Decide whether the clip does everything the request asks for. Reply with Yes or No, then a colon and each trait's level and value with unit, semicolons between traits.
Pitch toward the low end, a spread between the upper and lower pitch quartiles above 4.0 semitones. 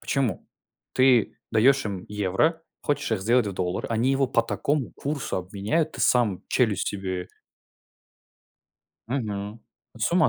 Yes: low, 115 Hz; average, 5.3 semitones